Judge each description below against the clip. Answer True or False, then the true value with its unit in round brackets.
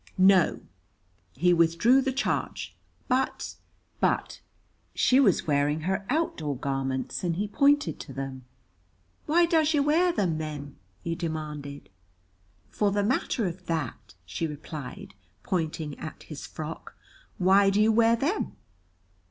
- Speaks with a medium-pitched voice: True (175 Hz)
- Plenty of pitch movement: True (7.5 semitones)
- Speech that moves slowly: True (130 wpm)